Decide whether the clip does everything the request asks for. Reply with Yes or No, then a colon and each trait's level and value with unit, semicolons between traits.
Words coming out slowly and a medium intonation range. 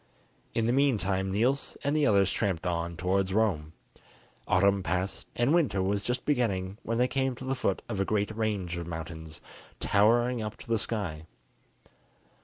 No: average, 170 wpm; average, 4.4 semitones